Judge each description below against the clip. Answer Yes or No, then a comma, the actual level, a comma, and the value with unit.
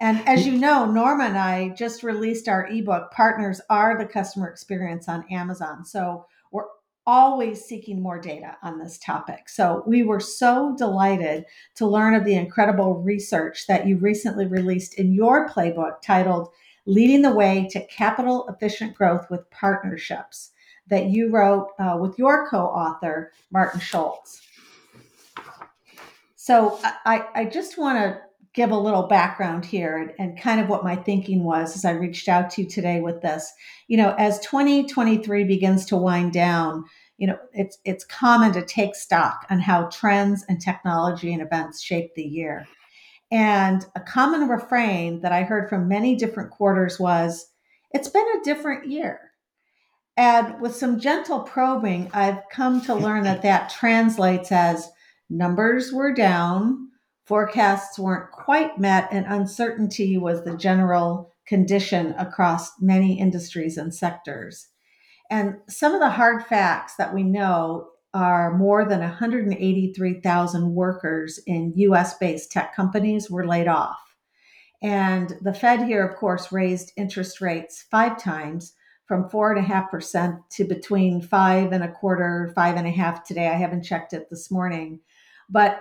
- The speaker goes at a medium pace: Yes, average, 155 wpm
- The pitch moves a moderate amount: Yes, average, 3.8 semitones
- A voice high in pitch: Yes, high, 195 Hz